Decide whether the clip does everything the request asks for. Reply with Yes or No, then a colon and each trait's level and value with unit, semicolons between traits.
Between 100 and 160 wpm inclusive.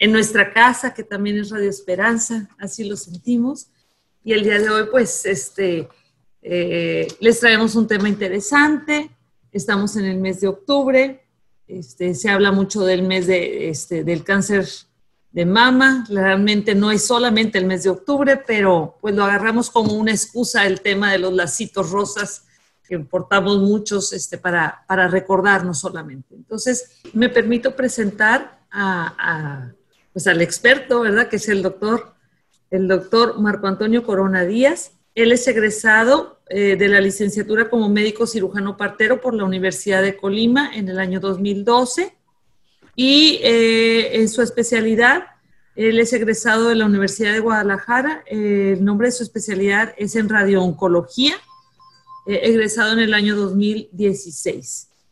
Yes: average, 150 wpm